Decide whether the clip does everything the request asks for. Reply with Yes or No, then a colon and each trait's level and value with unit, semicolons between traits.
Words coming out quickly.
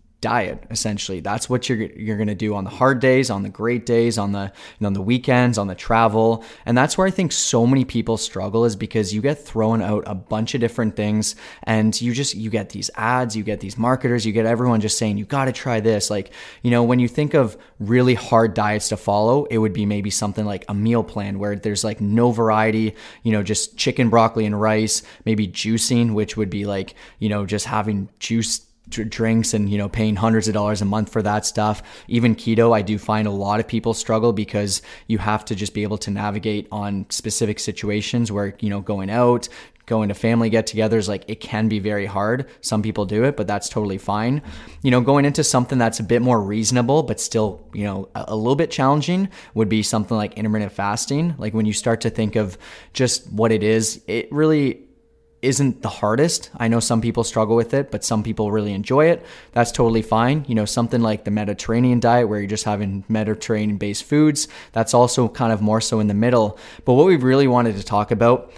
Yes: fast, 220 wpm